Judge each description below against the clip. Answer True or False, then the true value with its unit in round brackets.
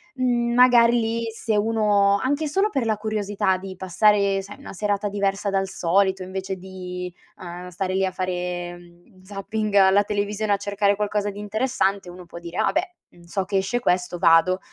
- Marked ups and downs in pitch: False (2.4 semitones)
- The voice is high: True (200 Hz)